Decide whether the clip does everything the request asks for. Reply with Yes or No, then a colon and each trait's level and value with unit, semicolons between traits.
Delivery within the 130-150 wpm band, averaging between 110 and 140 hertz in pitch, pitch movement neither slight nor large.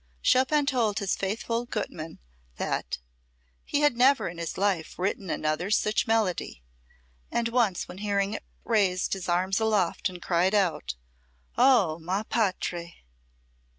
No: slow, 135 wpm; high, 200 Hz; average, 4.2 semitones